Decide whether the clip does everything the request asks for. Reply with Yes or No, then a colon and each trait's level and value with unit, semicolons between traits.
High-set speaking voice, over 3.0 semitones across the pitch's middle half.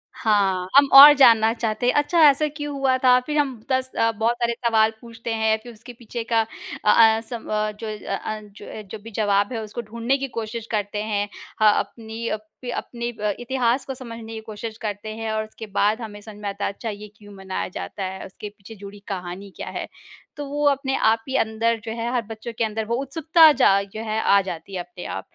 No: high, 220 Hz; narrow, 2.6 semitones